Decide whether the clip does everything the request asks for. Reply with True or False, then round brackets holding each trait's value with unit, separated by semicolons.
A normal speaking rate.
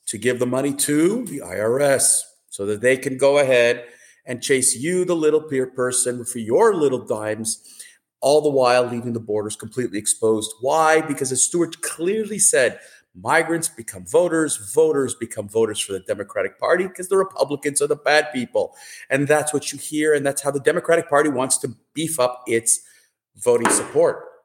True (180 wpm)